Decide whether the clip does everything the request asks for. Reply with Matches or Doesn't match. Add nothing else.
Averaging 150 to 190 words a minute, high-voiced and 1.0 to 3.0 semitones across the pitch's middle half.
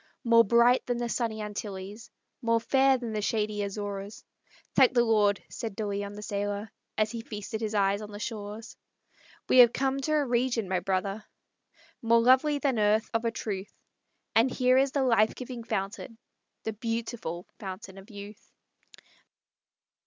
Matches